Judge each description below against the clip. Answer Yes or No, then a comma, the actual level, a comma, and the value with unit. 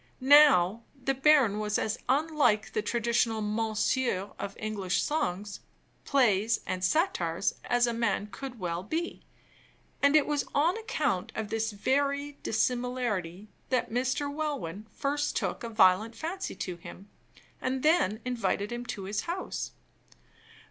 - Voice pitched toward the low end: No, high, 235 Hz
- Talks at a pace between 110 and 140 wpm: Yes, slow, 135 wpm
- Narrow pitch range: No, wide, 5.5 semitones